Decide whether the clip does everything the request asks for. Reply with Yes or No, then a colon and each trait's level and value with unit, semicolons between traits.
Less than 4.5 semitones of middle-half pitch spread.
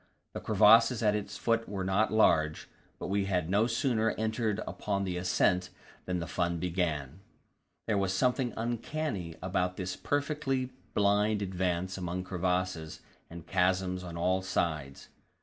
Yes: average, 3.4 semitones